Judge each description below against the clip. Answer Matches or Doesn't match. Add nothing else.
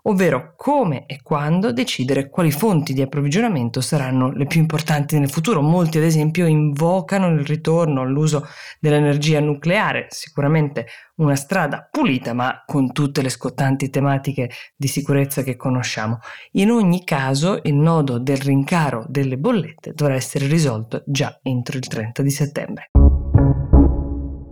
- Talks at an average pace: Matches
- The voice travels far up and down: Doesn't match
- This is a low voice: Doesn't match